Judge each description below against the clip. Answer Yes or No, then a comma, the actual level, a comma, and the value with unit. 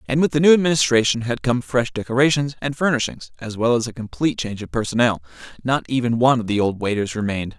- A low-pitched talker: Yes, low, 120 Hz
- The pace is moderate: No, fast, 215 wpm